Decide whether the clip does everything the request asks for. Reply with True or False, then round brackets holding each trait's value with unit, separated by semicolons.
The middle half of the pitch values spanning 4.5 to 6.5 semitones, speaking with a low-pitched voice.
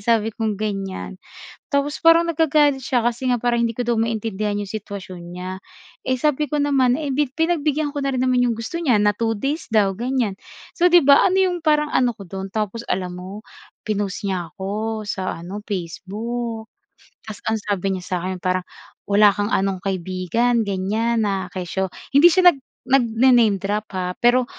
False (5.2 semitones; 225 Hz)